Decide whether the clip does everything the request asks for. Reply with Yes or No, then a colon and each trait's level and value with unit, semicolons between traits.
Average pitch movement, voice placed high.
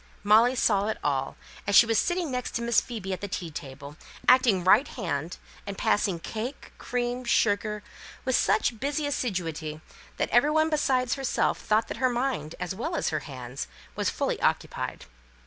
No: wide, 6.0 semitones; high, 220 Hz